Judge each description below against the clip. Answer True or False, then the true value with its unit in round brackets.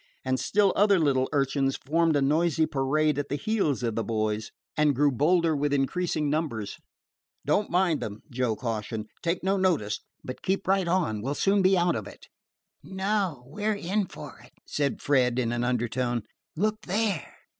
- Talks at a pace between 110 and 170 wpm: False (180 wpm)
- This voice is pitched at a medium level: True (145 Hz)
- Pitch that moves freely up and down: True (6.3 semitones)